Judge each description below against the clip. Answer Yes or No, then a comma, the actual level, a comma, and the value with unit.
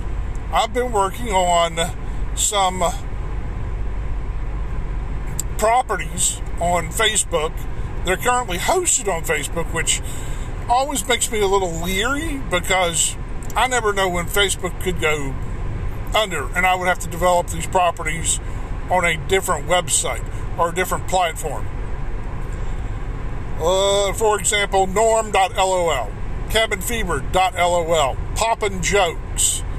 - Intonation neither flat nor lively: No, wide, 6.8 semitones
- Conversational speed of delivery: No, slow, 105 wpm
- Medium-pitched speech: Yes, medium, 180 Hz